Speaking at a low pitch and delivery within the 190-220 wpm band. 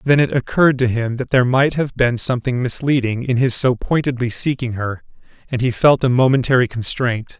Yes: low, 125 Hz; average, 195 wpm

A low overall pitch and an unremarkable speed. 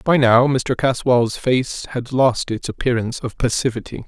Yes: low, 125 Hz; average, 160 wpm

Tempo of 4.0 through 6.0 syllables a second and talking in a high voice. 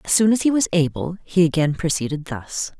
No: 5.5 syllables/s; medium, 170 Hz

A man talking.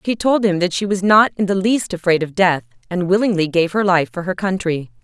No: female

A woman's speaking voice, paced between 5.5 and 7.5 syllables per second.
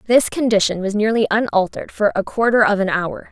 Yes: female; 5.8 syllables/s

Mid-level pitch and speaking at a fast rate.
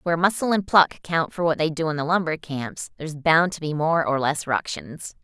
Yes: medium, 160 Hz; fast, 240 wpm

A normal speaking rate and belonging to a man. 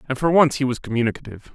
No: fast, 235 wpm; male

